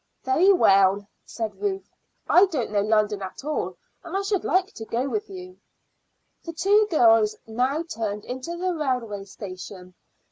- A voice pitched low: No, very high, 260 Hz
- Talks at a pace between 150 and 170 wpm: Yes, average, 155 wpm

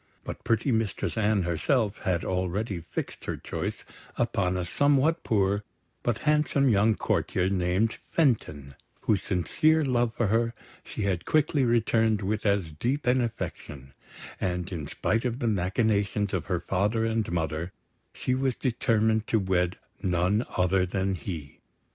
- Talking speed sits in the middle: Yes, average, 150 wpm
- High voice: No, low, 105 Hz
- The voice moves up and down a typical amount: Yes, average, 4.4 semitones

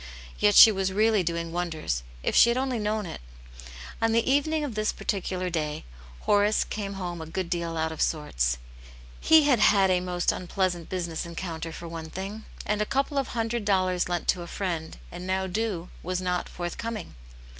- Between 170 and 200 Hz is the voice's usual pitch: Yes, medium, 185 Hz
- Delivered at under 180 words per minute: No, average, 190 wpm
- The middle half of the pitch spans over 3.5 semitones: Yes, average, 4.0 semitones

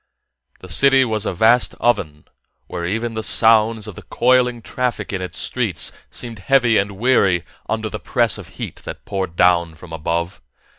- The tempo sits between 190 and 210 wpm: No, average, 175 wpm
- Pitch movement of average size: Yes, average, 4.8 semitones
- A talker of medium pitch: No, low, 110 Hz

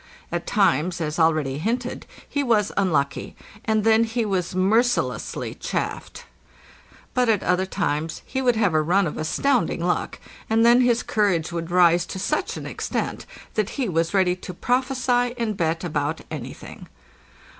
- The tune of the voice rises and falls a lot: Yes, wide, 5.7 semitones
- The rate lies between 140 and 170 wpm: Yes, average, 155 wpm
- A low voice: No, high, 195 Hz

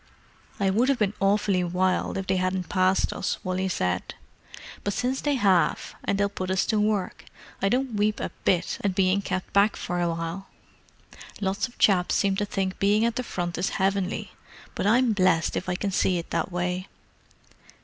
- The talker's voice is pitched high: Yes, high, 195 Hz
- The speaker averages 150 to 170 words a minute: No, average, 190 wpm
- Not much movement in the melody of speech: Yes, narrow, 2.1 semitones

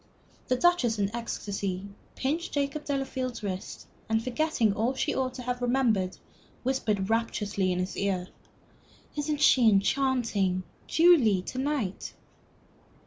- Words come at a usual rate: No, slow, 130 wpm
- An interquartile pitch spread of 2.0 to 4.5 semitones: No, average, 5.1 semitones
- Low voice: No, high, 235 Hz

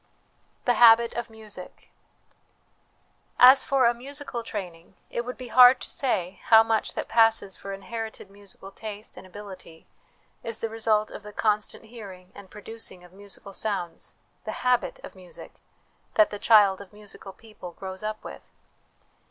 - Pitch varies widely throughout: No, average, 2.8 semitones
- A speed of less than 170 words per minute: Yes, average, 155 wpm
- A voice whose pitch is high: Yes, high, 215 Hz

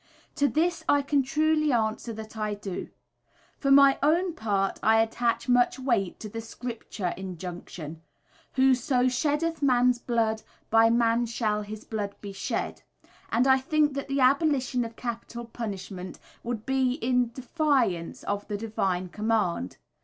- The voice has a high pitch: Yes, high, 235 Hz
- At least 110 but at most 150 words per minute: Yes, average, 145 wpm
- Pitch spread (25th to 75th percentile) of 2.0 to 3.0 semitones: No, average, 4.1 semitones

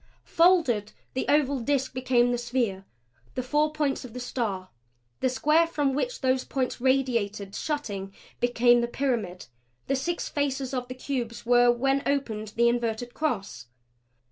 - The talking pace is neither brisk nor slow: Yes, average, 150 wpm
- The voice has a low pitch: No, very high, 250 Hz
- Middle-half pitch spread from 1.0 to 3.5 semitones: Yes, average, 3.0 semitones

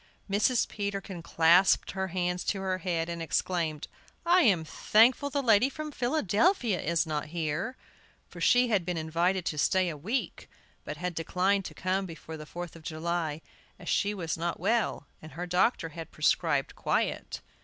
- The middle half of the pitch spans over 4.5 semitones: No, average, 3.8 semitones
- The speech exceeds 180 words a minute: No, average, 170 wpm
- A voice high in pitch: No, medium, 180 Hz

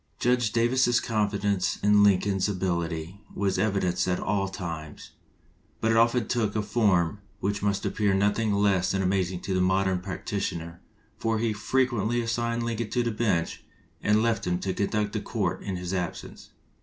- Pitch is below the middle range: Yes, low, 100 Hz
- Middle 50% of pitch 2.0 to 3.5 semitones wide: Yes, average, 3.2 semitones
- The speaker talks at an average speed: Yes, average, 170 wpm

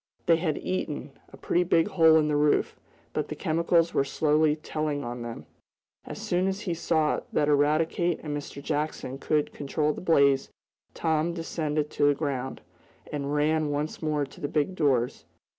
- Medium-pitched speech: Yes, medium, 150 Hz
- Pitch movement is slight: Yes, narrow, 2.0 semitones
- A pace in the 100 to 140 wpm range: No, average, 175 wpm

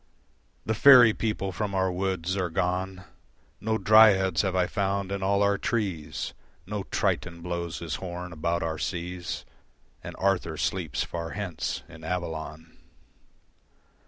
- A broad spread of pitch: No, average, 2.7 semitones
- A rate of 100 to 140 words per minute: Yes, slow, 135 wpm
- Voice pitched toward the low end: Yes, very low, 90 Hz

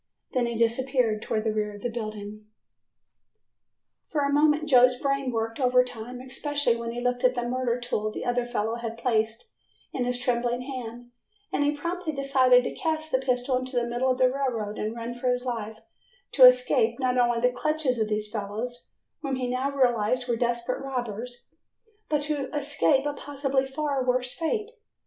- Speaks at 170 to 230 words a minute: Yes, average, 180 wpm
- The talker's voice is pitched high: Yes, very high, 250 Hz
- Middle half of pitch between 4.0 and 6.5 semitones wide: No, narrow, 2.6 semitones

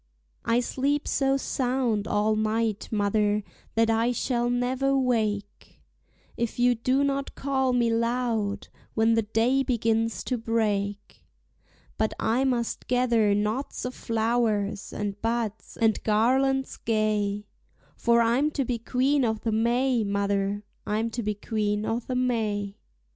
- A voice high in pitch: Yes, high, 230 Hz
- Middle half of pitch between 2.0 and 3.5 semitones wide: Yes, average, 2.9 semitones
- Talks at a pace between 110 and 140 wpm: Yes, slow, 135 wpm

